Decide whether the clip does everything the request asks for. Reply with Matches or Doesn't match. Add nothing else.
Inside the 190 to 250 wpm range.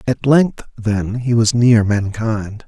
Doesn't match